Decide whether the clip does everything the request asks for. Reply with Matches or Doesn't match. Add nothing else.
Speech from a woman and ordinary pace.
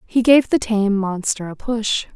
Matches